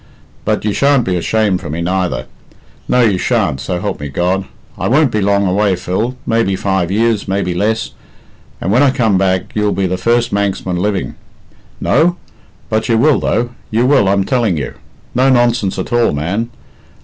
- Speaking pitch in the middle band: No, low, 100 Hz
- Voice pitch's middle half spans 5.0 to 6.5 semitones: No, average, 4.0 semitones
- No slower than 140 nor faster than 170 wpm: No, average, 185 wpm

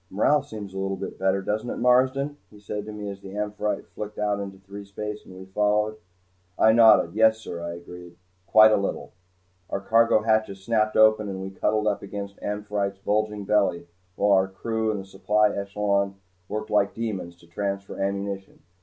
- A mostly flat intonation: Yes, narrow, 1.7 semitones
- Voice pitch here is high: No, low, 105 Hz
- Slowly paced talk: No, average, 180 wpm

